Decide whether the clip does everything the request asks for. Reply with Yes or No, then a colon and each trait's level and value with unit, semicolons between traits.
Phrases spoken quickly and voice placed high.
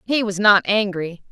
No: average, 185 wpm; high, 200 Hz